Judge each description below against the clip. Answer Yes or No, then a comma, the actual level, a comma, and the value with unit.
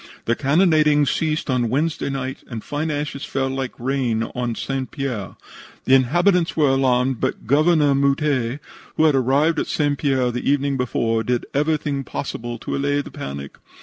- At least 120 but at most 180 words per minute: Yes, average, 165 wpm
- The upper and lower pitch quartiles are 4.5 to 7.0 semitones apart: No, average, 2.8 semitones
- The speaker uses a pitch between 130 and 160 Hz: Yes, low, 135 Hz